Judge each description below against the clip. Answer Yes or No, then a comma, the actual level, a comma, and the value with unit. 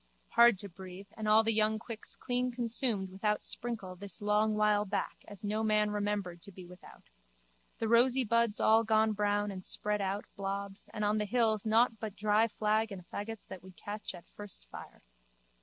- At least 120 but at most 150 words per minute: No, average, 190 wpm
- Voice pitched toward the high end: Yes, high, 210 Hz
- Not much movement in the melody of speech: Yes, narrow, 1.8 semitones